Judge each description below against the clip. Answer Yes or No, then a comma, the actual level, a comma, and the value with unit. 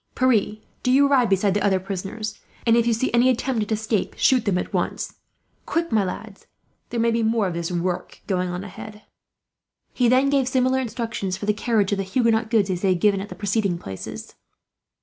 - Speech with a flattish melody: No, average, 3.5 semitones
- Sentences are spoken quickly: Yes, fast, 210 wpm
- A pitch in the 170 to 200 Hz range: No, high, 215 Hz